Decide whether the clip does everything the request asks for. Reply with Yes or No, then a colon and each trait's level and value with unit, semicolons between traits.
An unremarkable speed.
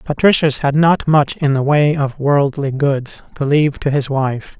Yes: average, 195 wpm